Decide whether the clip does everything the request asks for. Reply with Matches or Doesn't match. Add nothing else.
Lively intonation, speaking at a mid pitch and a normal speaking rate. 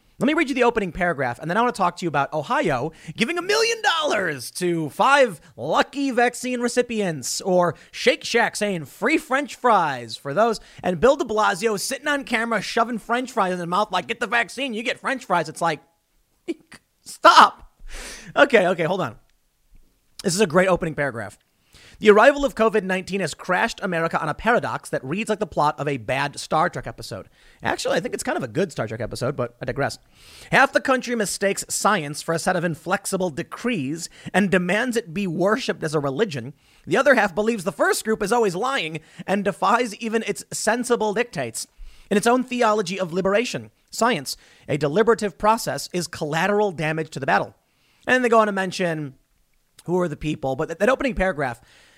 Doesn't match